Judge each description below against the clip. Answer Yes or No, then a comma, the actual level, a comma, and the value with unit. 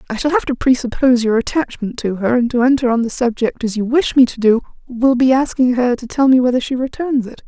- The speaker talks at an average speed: No, fast, 255 wpm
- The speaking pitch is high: Yes, very high, 250 Hz